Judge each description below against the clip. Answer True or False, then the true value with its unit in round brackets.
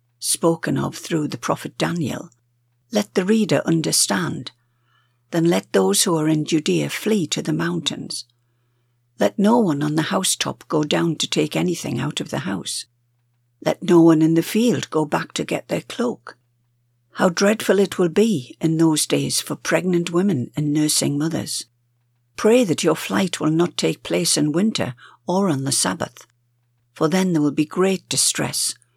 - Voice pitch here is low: False (155 Hz)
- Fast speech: False (170 wpm)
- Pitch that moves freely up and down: True (6.3 semitones)